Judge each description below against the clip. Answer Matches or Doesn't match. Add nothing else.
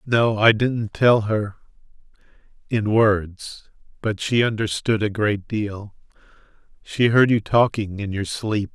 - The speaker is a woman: Doesn't match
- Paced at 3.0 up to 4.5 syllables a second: Matches